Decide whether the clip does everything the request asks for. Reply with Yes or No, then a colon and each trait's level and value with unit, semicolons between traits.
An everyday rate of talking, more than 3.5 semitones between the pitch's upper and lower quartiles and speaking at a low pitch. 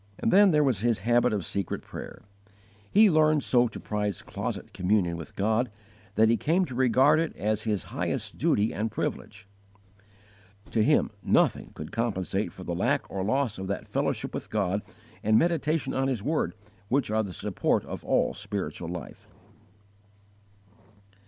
Yes: average, 150 wpm; average, 5.2 semitones; low, 110 Hz